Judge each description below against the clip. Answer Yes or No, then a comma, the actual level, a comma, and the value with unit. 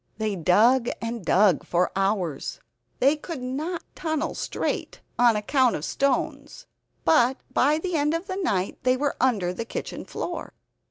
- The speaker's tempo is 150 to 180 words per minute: Yes, average, 155 wpm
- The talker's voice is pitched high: Yes, very high, 255 Hz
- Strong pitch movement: Yes, wide, 6.5 semitones